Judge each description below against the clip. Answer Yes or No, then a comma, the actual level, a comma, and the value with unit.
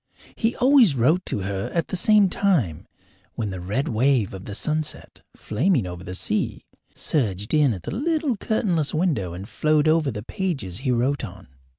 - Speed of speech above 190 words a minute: No, average, 180 wpm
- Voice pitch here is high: No, medium, 140 Hz